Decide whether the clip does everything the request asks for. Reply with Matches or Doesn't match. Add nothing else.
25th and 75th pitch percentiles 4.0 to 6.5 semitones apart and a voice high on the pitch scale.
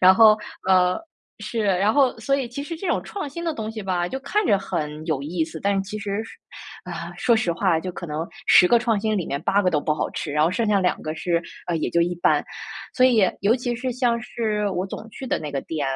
Matches